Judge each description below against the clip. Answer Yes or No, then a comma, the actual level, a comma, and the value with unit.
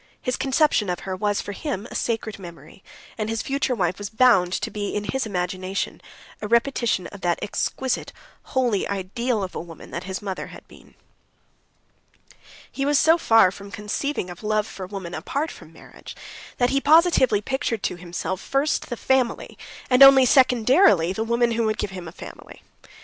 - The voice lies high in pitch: Yes, high, 215 Hz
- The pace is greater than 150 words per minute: Yes, average, 180 wpm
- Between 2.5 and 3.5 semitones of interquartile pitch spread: No, average, 5.3 semitones